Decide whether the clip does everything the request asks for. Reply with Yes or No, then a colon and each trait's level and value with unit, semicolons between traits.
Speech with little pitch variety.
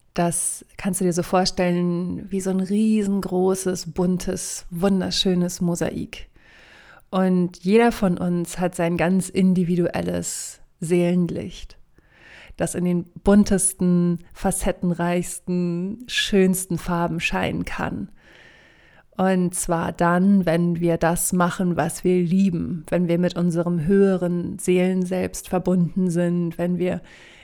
Yes: narrow, 1.4 semitones